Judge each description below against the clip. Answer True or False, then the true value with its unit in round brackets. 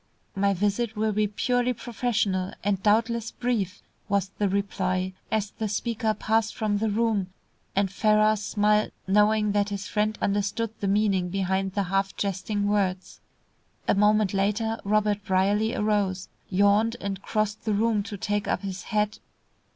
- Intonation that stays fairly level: True (1.6 semitones)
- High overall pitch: True (205 Hz)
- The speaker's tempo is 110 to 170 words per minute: True (150 wpm)